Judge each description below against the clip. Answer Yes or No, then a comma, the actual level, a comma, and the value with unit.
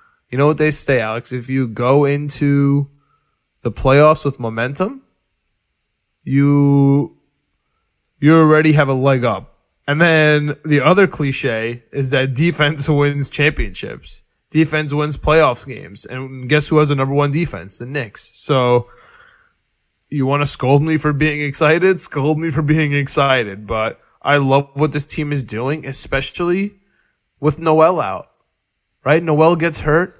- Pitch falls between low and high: Yes, medium, 145 Hz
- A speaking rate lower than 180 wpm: Yes, average, 150 wpm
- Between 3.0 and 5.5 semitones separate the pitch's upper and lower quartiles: No, narrow, 2.5 semitones